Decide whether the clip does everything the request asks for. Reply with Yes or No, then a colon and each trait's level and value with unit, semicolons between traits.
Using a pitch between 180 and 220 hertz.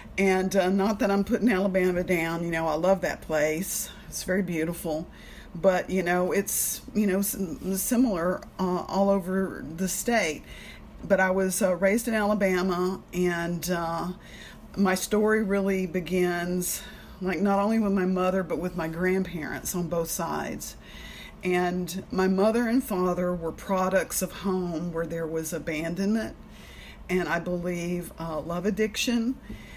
Yes: medium, 185 Hz